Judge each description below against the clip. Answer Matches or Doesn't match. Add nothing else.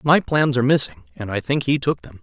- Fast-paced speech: Matches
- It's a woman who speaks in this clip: Doesn't match